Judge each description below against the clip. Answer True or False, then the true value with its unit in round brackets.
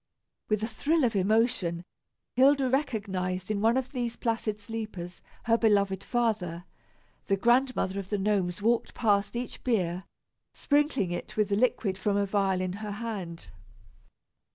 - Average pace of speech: True (150 wpm)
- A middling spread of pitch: True (3.8 semitones)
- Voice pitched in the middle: False (210 Hz)